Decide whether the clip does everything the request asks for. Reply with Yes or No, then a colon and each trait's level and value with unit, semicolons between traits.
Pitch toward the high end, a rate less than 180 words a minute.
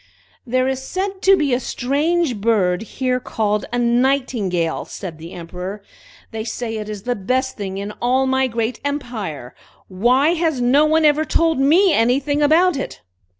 Yes: very high, 250 Hz; average, 165 wpm